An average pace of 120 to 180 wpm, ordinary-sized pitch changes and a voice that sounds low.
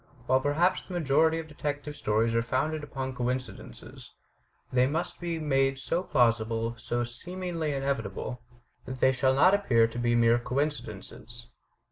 Yes: average, 145 wpm; average, 4.3 semitones; low, 130 Hz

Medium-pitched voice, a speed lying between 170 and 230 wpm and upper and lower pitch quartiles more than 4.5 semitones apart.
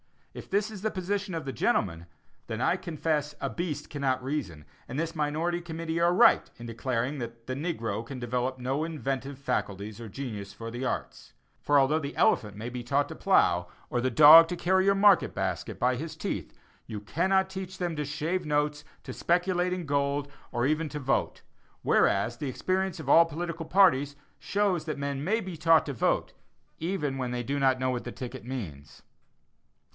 Yes: medium, 145 Hz; average, 190 wpm; average, 5.2 semitones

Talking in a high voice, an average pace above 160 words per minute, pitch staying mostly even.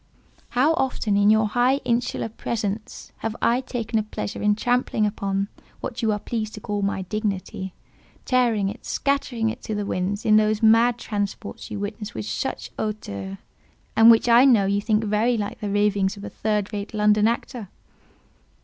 Yes: high, 215 Hz; average, 175 wpm; narrow, 2.3 semitones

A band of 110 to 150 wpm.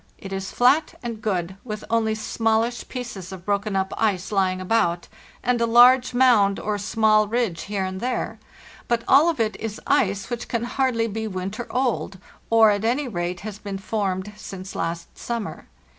No: average, 175 wpm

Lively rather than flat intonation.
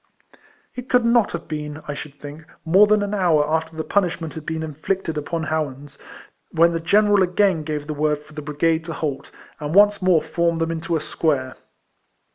No: average, 3.4 semitones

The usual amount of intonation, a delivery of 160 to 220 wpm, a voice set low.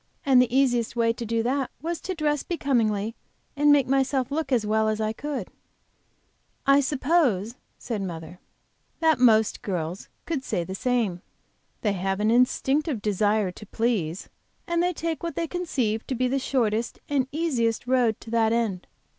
No: average, 4.5 semitones; average, 170 wpm; high, 240 Hz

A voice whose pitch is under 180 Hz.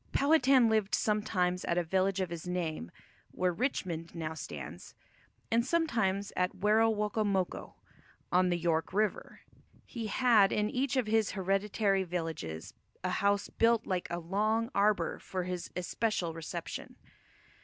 No: high, 195 Hz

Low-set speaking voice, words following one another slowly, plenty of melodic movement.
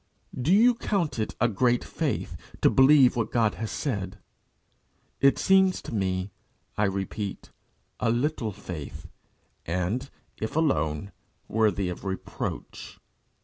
Yes: low, 110 Hz; slow, 125 wpm; wide, 6.2 semitones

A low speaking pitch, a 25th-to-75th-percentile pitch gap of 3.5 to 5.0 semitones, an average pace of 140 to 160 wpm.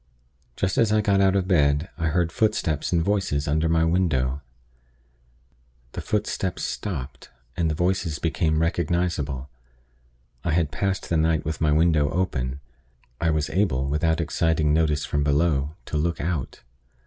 No: very low, 80 Hz; average, 3.1 semitones; average, 150 wpm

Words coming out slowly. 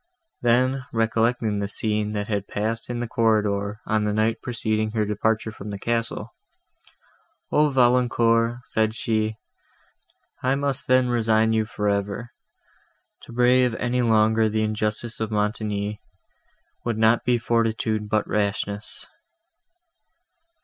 Yes: slow, 130 wpm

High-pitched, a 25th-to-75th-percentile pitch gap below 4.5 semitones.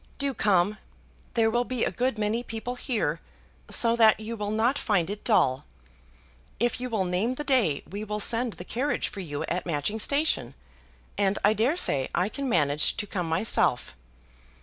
No: high, 215 Hz; average, 5.1 semitones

